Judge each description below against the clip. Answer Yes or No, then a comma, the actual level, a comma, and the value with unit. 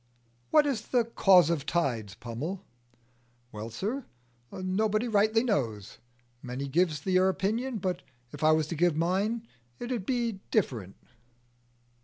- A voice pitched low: No, medium, 185 Hz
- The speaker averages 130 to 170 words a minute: Yes, average, 140 wpm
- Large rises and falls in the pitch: Yes, wide, 6.9 semitones